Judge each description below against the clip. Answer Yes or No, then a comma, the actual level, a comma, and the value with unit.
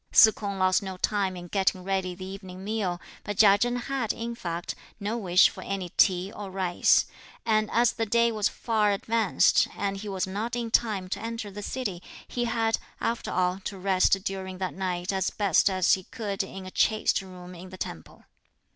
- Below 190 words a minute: No, average, 195 wpm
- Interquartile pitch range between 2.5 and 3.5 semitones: Yes, average, 2.8 semitones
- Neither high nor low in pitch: No, high, 195 Hz